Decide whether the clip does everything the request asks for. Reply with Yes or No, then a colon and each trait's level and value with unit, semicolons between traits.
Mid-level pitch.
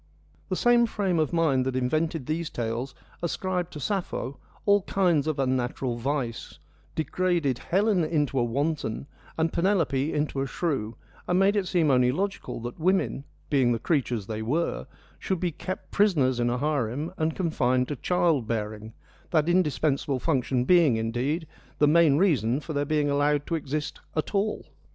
Yes: medium, 150 Hz